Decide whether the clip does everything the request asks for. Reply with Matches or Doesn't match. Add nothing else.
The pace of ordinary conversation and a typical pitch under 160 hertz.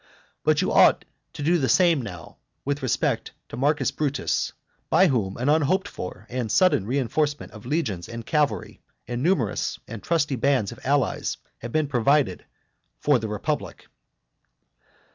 Matches